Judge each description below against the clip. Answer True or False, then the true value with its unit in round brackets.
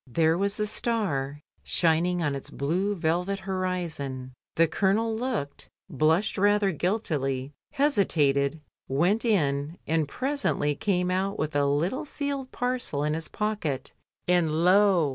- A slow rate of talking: True (130 wpm)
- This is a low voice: False (175 Hz)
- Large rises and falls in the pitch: True (5.8 semitones)